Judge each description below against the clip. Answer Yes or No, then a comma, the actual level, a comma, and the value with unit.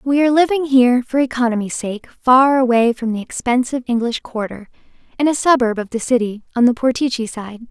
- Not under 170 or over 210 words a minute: Yes, average, 185 wpm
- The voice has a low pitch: No, high, 245 Hz